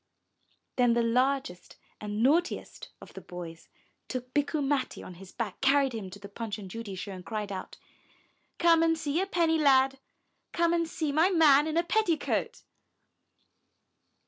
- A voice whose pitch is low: No, very high, 265 Hz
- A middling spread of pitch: No, wide, 7.4 semitones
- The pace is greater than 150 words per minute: Yes, average, 165 wpm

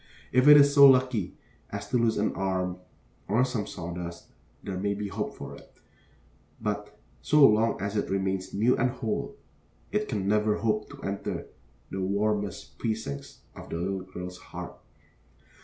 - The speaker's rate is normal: Yes, average, 160 wpm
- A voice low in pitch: Yes, low, 105 Hz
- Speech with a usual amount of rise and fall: Yes, average, 3.4 semitones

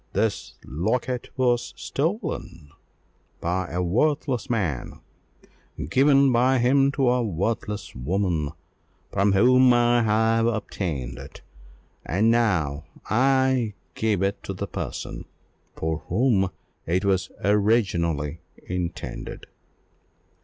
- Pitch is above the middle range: No, low, 110 Hz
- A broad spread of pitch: Yes, wide, 5.8 semitones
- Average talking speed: No, slow, 105 wpm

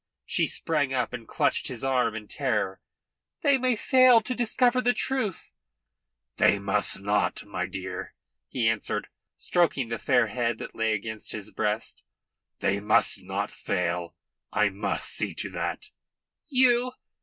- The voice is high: No, low, 120 Hz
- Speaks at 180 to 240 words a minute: No, average, 155 wpm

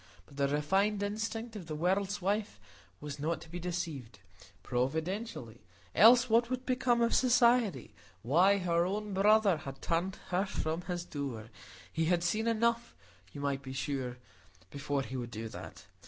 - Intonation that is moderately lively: No, wide, 7.1 semitones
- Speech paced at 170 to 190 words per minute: No, average, 155 wpm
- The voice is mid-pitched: Yes, medium, 175 Hz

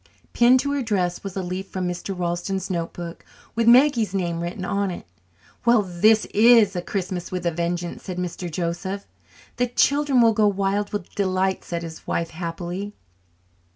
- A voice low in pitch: No, high, 190 Hz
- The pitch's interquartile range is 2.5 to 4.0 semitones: Yes, average, 3.4 semitones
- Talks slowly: No, average, 165 wpm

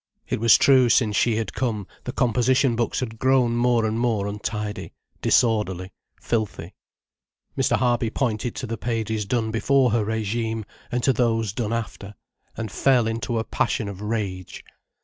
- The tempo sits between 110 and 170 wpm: Yes, average, 160 wpm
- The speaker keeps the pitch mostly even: Yes, narrow, 2.2 semitones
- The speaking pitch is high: No, low, 115 Hz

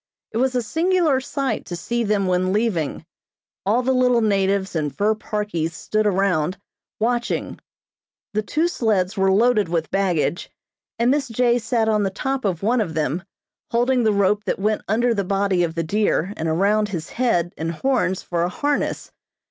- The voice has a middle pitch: No, high, 210 Hz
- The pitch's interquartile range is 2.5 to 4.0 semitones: No, average, 4.7 semitones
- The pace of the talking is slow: No, average, 180 wpm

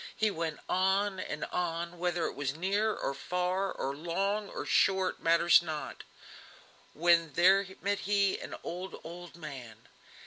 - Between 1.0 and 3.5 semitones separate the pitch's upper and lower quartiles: Yes, average, 2.9 semitones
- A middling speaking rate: Yes, average, 145 wpm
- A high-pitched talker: No, medium, 175 Hz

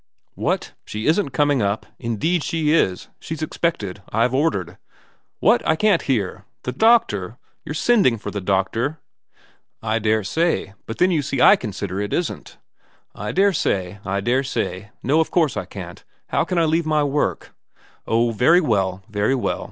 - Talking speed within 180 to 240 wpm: Yes, average, 185 wpm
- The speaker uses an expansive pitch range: Yes, wide, 7.7 semitones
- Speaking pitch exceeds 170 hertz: No, low, 125 Hz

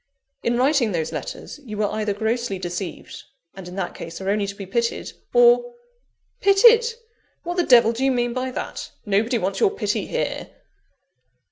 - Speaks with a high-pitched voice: Yes, high, 235 Hz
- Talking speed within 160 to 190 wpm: Yes, average, 175 wpm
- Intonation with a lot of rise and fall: Yes, wide, 7.1 semitones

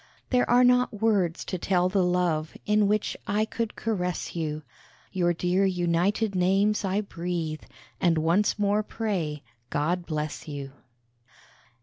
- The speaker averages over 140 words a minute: No, slow, 135 wpm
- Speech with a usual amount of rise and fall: Yes, average, 3.8 semitones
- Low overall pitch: No, medium, 180 Hz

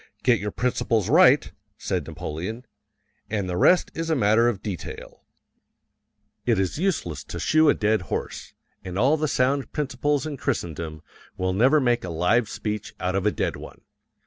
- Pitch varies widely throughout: Yes, wide, 6.8 semitones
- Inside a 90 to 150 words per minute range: No, average, 170 wpm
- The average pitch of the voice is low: Yes, low, 110 Hz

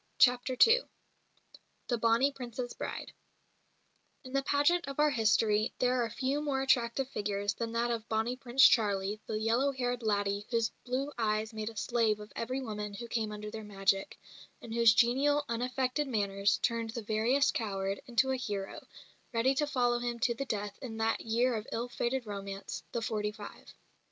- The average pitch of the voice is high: Yes, high, 230 Hz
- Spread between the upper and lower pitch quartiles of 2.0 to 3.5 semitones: Yes, average, 3.2 semitones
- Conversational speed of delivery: Yes, average, 175 wpm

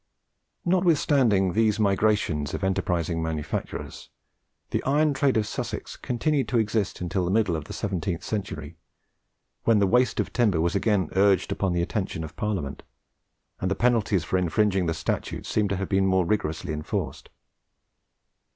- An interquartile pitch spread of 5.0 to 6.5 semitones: No, average, 4.2 semitones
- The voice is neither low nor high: No, very low, 95 Hz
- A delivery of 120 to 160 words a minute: Yes, average, 155 wpm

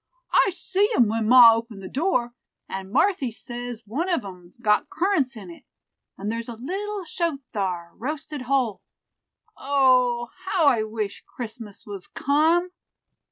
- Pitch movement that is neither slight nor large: No, wide, 5.9 semitones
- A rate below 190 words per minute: Yes, average, 150 wpm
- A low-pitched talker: No, high, 245 Hz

